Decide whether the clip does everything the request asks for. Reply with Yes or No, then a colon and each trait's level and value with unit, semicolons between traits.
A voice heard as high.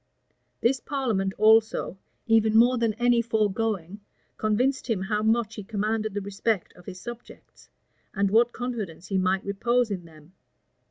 Yes: high, 215 Hz